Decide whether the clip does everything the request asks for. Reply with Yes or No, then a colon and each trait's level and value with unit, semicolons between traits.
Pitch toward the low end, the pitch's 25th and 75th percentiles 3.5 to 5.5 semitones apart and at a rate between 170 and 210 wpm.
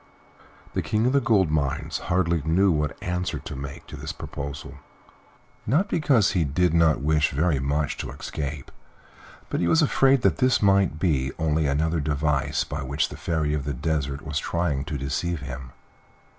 Yes: very low, 75 Hz; average, 3.9 semitones; average, 175 wpm